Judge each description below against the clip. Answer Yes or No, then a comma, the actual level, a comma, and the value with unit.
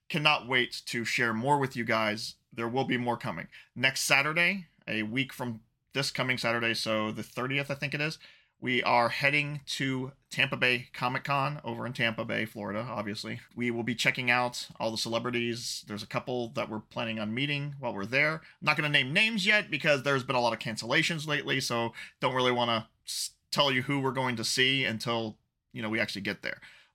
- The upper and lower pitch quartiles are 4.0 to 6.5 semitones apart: No, average, 3.3 semitones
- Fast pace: Yes, fast, 210 wpm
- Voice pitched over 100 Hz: Yes, low, 125 Hz